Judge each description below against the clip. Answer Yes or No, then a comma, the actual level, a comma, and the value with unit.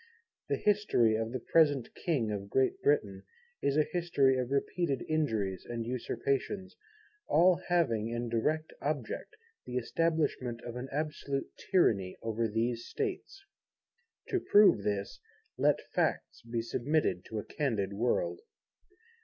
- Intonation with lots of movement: Yes, wide, 5.7 semitones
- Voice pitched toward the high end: No, low, 130 Hz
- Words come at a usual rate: No, slow, 130 wpm